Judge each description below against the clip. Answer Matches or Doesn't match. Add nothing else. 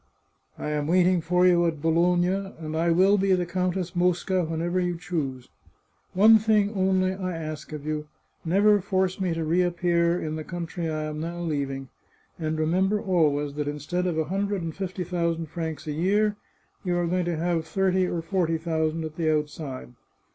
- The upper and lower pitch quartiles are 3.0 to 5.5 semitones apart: Doesn't match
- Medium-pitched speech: Matches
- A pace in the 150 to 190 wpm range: Matches